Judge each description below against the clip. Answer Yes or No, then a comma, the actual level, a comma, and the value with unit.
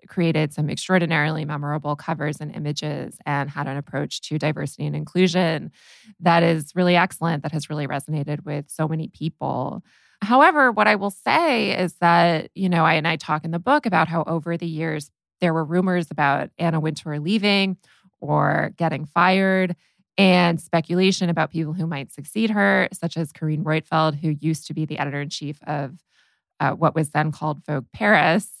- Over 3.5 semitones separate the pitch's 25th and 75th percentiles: No, average, 3.0 semitones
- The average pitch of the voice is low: No, medium, 160 Hz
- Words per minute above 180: No, average, 175 wpm